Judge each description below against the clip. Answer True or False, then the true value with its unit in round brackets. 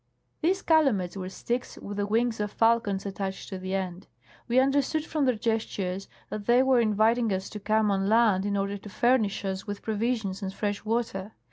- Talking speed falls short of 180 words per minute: False (195 wpm)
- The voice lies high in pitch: True (210 Hz)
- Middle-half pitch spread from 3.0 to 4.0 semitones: True (3.4 semitones)